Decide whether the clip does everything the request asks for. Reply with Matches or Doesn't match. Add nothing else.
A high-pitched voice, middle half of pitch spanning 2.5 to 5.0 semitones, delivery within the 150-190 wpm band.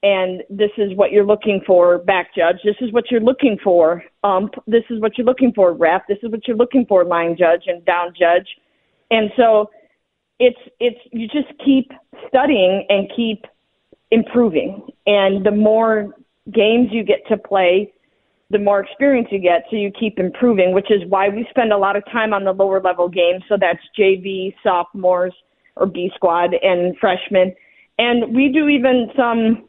Matches